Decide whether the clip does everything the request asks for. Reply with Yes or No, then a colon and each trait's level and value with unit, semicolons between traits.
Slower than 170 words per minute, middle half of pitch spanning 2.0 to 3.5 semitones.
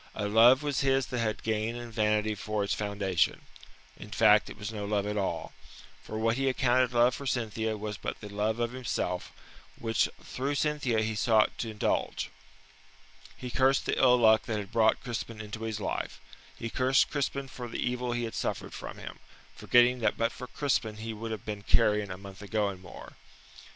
No: average, 195 wpm; average, 2.7 semitones